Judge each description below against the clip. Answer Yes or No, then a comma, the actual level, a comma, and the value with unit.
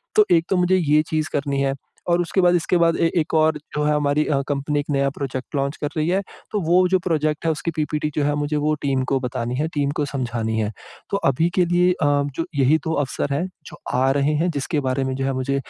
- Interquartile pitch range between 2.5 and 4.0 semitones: Yes, average, 3.1 semitones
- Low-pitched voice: No, medium, 150 Hz